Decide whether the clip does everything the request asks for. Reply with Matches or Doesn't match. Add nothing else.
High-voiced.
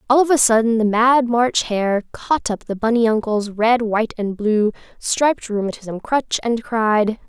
Matches